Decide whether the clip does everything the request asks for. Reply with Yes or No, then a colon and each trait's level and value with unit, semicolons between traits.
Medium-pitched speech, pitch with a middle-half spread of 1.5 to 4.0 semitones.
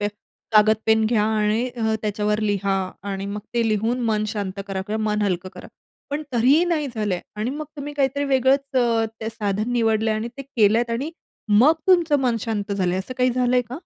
No: high, 220 Hz; average, 3.4 semitones